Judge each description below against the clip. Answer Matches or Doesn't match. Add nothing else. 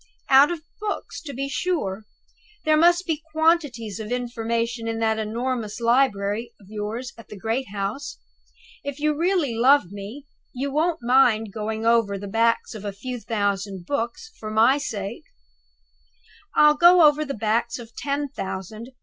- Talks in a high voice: Matches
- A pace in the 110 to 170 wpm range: Matches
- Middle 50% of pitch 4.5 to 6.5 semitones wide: Matches